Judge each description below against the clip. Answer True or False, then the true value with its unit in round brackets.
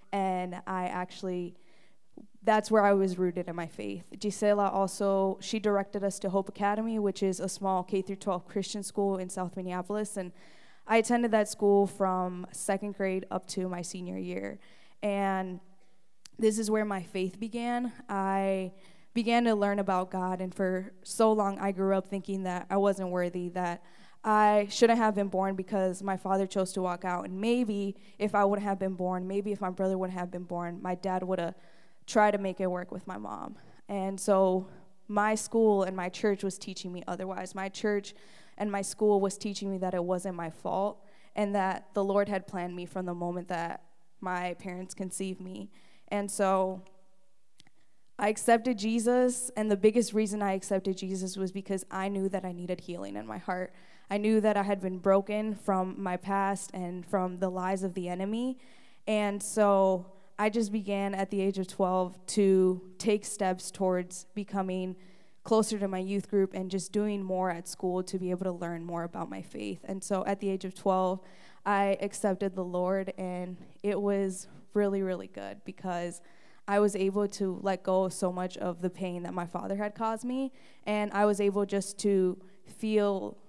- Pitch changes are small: True (1.8 semitones)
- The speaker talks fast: False (190 wpm)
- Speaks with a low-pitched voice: False (195 Hz)